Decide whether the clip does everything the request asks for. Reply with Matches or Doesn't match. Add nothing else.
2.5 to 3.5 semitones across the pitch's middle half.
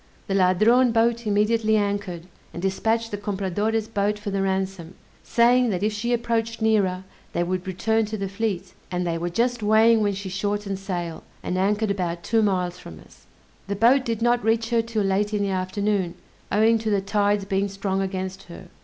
Matches